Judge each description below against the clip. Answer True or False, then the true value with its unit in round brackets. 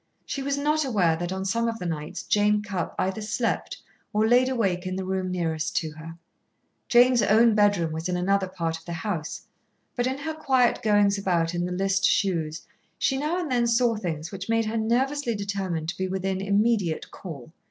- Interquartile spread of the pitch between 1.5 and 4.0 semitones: False (4.8 semitones)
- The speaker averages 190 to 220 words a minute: True (200 wpm)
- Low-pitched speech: False (200 Hz)